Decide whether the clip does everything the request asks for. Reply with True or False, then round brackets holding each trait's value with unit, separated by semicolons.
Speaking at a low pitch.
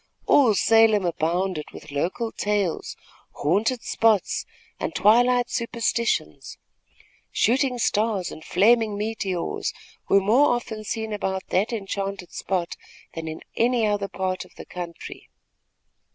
False (205 Hz)